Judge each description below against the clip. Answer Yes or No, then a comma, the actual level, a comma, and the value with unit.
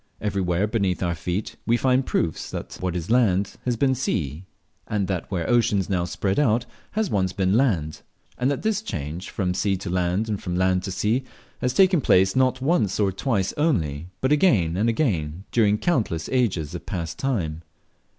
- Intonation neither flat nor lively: No, wide, 5.8 semitones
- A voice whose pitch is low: Yes, low, 100 Hz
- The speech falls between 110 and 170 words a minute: No, average, 185 wpm